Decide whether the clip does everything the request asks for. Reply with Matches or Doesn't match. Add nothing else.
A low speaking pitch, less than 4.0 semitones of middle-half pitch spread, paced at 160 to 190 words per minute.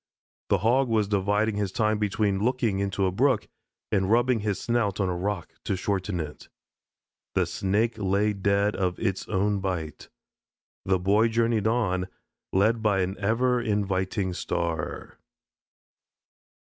Doesn't match